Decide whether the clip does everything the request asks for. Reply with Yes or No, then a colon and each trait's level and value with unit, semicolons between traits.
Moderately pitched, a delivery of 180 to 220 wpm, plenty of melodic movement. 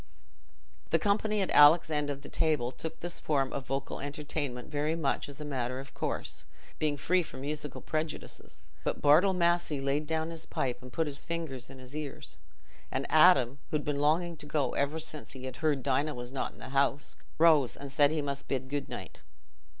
No: medium, 145 Hz; fast, 205 wpm; average, 2.7 semitones